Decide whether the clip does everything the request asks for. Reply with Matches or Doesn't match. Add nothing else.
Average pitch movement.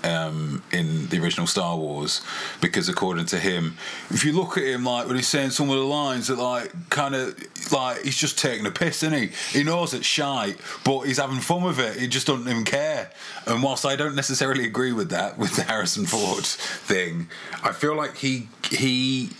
Matches